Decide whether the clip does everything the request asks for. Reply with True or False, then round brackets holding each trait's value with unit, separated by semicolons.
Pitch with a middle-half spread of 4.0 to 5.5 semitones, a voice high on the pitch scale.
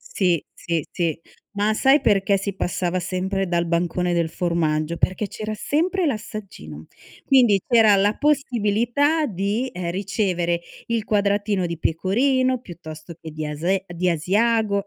True (4.3 semitones; 195 Hz)